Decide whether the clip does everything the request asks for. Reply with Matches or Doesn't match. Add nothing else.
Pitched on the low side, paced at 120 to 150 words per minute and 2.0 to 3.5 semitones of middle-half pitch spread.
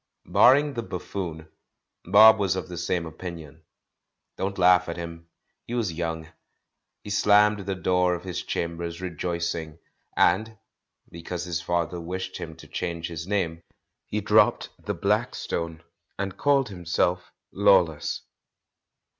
Matches